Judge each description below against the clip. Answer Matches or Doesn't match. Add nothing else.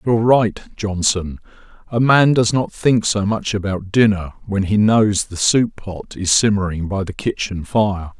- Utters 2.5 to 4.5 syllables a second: Matches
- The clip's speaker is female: Doesn't match